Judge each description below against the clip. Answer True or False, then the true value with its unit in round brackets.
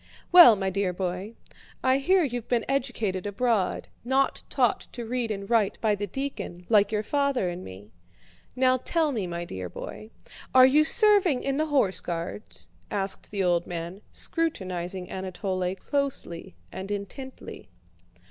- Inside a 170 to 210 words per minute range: False (150 wpm)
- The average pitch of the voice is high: True (210 Hz)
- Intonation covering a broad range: True (6.1 semitones)